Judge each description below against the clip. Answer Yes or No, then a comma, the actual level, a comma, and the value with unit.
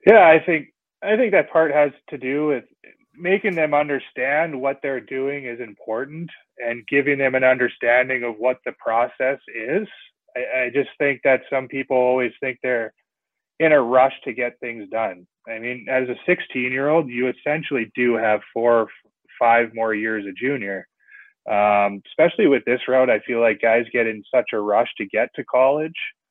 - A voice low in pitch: Yes, low, 130 Hz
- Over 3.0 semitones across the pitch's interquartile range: Yes, average, 3.4 semitones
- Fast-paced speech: No, average, 185 wpm